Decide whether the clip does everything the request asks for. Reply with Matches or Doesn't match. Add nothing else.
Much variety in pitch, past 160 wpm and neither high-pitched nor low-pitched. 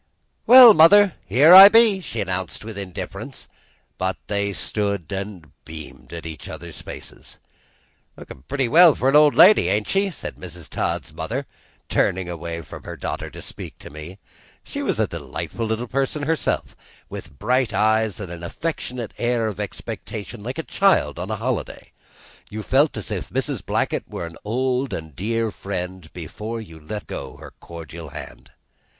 Doesn't match